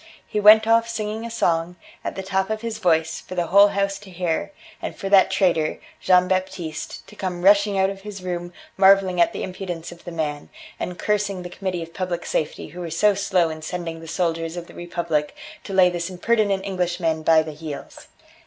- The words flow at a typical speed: No, fast, 210 wpm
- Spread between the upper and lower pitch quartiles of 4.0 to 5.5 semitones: No, average, 2.8 semitones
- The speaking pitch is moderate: Yes, medium, 180 Hz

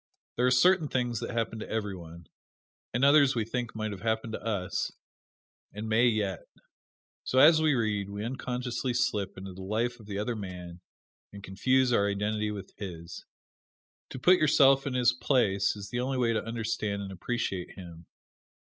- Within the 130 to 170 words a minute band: No, average, 180 wpm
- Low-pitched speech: Yes, low, 110 Hz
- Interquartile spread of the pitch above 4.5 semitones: No, average, 3.7 semitones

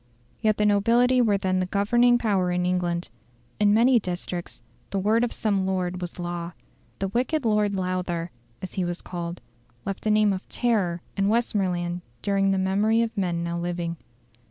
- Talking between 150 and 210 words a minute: Yes, average, 175 wpm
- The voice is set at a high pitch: Yes, high, 195 Hz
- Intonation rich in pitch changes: No, average, 3.3 semitones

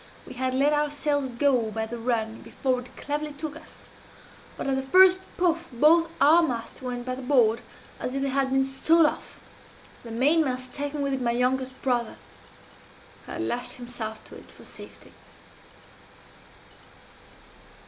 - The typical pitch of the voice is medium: No, very high, 265 Hz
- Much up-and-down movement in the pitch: No, average, 3.2 semitones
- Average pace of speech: Yes, average, 165 wpm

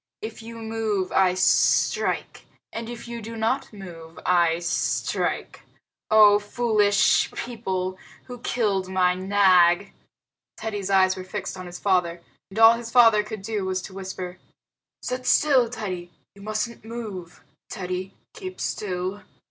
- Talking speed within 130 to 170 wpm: Yes, average, 140 wpm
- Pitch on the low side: No, high, 205 Hz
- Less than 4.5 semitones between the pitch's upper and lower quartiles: Yes, average, 3.4 semitones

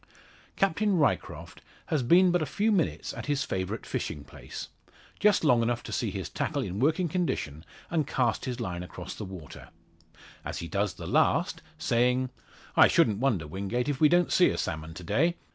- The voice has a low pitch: Yes, low, 125 Hz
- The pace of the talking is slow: No, average, 185 wpm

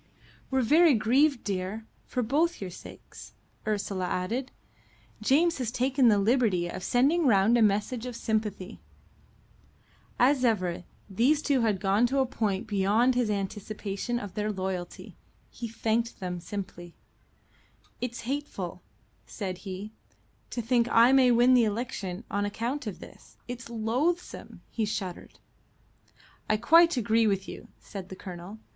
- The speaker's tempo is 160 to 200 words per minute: No, average, 140 wpm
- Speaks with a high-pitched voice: Yes, high, 225 Hz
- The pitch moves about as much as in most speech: Yes, average, 4.1 semitones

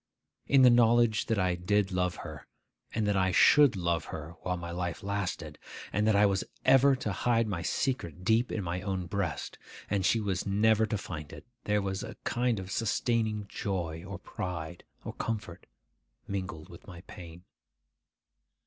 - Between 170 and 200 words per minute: Yes, average, 175 wpm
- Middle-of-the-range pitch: No, low, 100 Hz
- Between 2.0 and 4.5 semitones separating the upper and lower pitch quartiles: Yes, average, 3.7 semitones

